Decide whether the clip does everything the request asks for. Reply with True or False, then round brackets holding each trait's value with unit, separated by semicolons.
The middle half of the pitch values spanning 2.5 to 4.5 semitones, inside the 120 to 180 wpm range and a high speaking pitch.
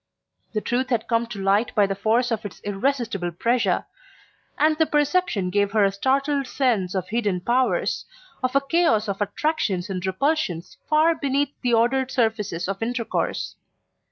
False (5.4 semitones; 160 wpm; 230 Hz)